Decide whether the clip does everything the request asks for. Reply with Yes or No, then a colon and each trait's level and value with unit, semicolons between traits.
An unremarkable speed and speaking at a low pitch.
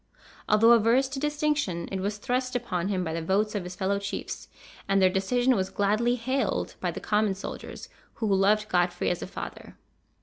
No: average, 190 wpm; high, 205 Hz